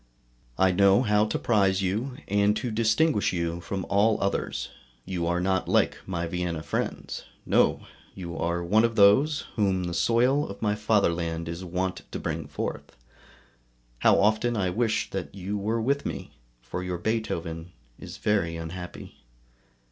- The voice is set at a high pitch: No, very low, 95 Hz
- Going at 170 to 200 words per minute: No, average, 155 wpm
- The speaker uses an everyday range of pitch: Yes, average, 3.7 semitones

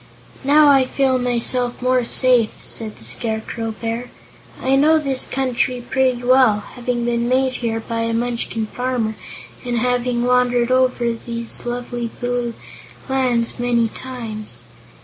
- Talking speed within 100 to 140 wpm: Yes, slow, 135 wpm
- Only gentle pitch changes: Yes, narrow, 1.6 semitones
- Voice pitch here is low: No, high, 245 Hz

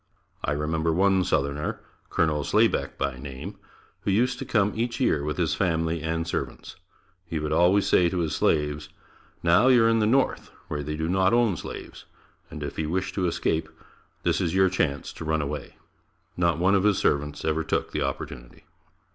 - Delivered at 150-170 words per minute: No, average, 190 wpm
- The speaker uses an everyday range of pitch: Yes, average, 4.1 semitones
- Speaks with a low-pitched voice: Yes, very low, 85 Hz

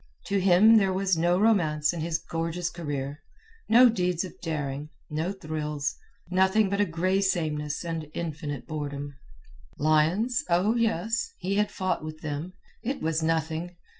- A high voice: No, medium, 170 Hz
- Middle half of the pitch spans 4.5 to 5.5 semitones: No, average, 3.8 semitones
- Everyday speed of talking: Yes, average, 145 wpm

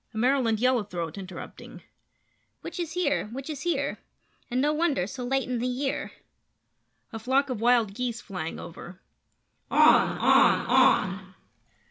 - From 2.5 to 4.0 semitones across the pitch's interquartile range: No, average, 4.9 semitones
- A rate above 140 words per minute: No, slow, 135 wpm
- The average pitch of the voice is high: Yes, high, 245 Hz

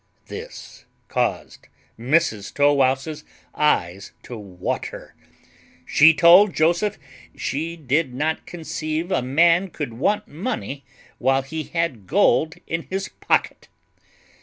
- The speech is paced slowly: Yes, slow, 110 wpm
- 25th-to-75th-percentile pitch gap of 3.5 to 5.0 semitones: Yes, average, 4.2 semitones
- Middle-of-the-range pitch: Yes, medium, 155 Hz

